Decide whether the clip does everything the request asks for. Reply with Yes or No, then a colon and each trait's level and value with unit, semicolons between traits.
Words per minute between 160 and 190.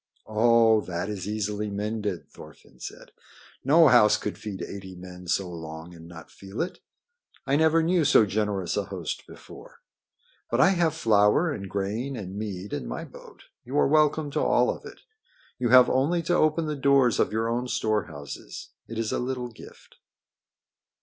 Yes: average, 175 wpm